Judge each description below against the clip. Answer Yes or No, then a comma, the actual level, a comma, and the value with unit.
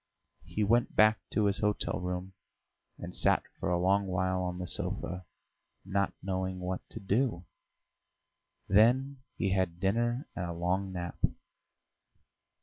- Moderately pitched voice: No, very low, 95 Hz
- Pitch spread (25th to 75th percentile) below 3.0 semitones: Yes, narrow, 2.6 semitones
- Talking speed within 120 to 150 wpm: Yes, average, 140 wpm